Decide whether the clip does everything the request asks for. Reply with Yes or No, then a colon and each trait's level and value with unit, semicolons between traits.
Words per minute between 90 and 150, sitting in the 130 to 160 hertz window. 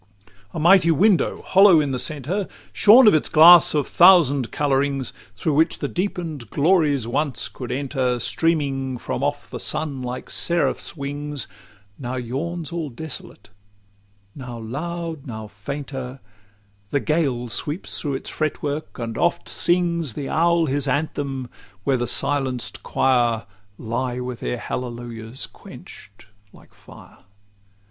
Yes: slow, 135 wpm; medium, 140 Hz